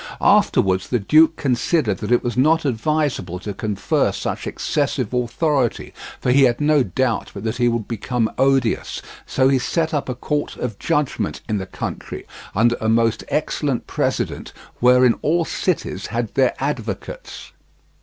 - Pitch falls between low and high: No, low, 125 Hz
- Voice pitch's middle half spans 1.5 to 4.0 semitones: No, average, 4.6 semitones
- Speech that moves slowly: No, average, 155 wpm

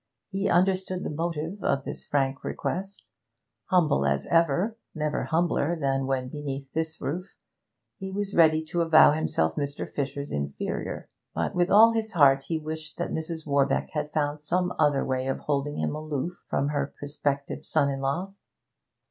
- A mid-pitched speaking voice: Yes, medium, 150 Hz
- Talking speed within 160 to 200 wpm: Yes, average, 165 wpm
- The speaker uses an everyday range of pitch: Yes, average, 3.7 semitones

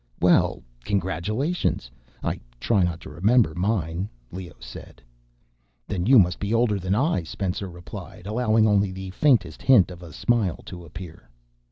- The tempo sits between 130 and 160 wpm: Yes, average, 150 wpm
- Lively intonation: No, average, 3.9 semitones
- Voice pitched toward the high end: No, very low, 95 Hz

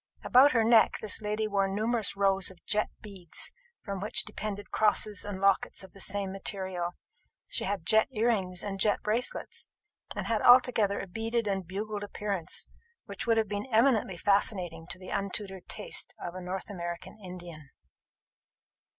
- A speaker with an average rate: Yes, average, 160 wpm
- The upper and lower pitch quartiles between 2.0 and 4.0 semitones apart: Yes, narrow, 2.4 semitones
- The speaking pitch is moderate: No, high, 200 Hz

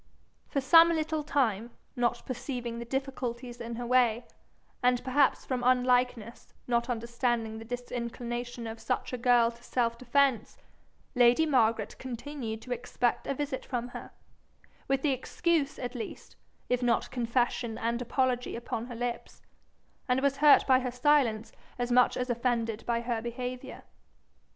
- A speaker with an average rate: Yes, average, 145 wpm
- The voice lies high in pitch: Yes, high, 245 Hz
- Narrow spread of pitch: Yes, narrow, 1.7 semitones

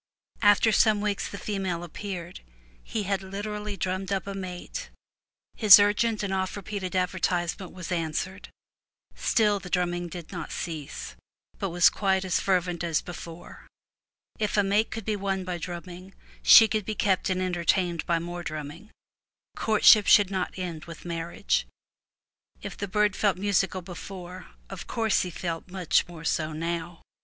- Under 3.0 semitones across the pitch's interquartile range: Yes, narrow, 2.6 semitones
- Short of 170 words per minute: Yes, average, 160 wpm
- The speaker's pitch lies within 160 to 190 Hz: Yes, medium, 185 Hz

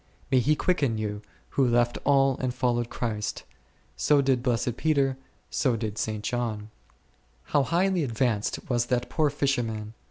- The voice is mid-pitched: No, low, 125 Hz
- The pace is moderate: Yes, average, 150 wpm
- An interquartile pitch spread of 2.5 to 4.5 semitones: Yes, average, 3.6 semitones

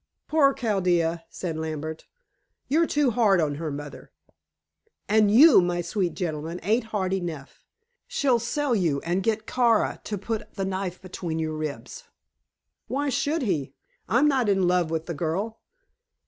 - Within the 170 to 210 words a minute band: No, average, 150 wpm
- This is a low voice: No, high, 190 Hz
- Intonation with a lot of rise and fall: Yes, wide, 6.0 semitones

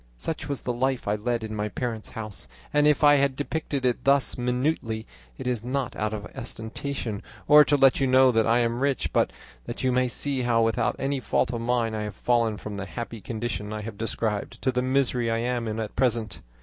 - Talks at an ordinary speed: No, fast, 225 wpm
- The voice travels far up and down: No, average, 3.1 semitones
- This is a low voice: Yes, low, 120 Hz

